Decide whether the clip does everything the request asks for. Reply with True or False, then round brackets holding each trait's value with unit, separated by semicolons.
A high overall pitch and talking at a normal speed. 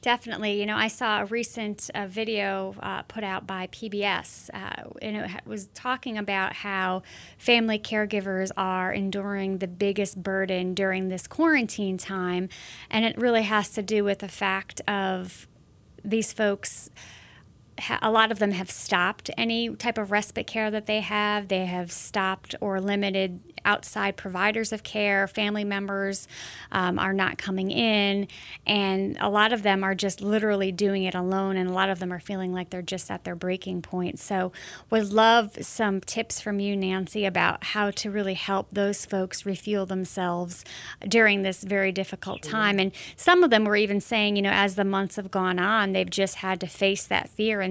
True (200 Hz; 180 wpm)